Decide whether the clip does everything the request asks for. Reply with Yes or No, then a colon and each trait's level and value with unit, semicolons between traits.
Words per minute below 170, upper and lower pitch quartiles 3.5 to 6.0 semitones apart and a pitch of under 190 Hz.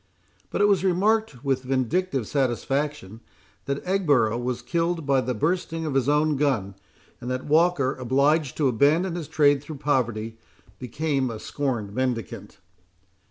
Yes: average, 145 wpm; average, 4.0 semitones; medium, 140 Hz